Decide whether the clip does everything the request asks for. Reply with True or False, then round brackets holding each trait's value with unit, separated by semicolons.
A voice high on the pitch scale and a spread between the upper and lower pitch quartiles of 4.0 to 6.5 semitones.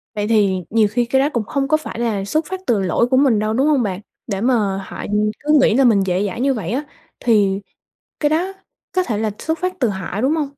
True (230 Hz; 5.1 semitones)